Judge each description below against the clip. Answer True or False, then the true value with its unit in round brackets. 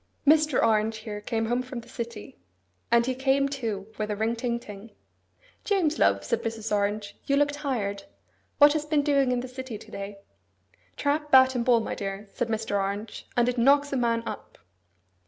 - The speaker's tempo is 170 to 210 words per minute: True (190 wpm)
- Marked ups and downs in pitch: False (4.3 semitones)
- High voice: True (235 Hz)